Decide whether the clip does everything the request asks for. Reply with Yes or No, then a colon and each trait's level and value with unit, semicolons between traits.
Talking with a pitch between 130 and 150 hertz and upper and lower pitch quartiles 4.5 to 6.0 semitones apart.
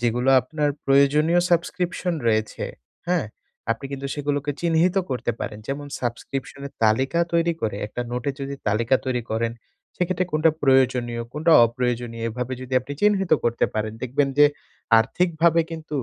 Yes: low, 135 Hz; average, 5.2 semitones